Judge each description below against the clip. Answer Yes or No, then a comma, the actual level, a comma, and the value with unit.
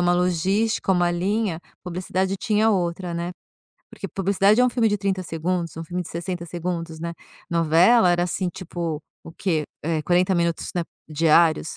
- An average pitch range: No, narrow, 2.3 semitones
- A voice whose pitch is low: No, medium, 175 Hz